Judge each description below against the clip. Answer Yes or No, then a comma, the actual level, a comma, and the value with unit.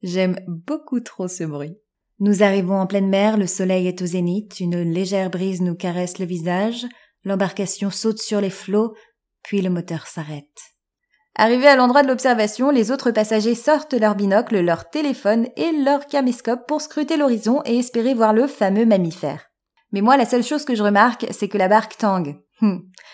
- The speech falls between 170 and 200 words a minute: Yes, average, 180 wpm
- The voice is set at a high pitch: Yes, high, 210 Hz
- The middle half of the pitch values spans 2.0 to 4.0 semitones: No, average, 4.5 semitones